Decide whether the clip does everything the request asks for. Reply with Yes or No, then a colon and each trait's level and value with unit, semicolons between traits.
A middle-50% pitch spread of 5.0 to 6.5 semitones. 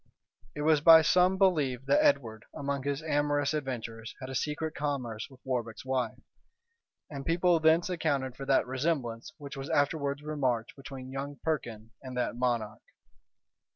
No: average, 3.3 semitones